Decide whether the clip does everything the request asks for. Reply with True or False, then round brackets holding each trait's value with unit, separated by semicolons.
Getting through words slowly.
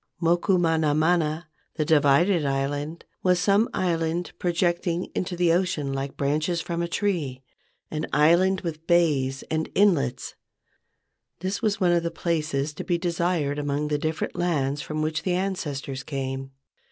False (150 wpm)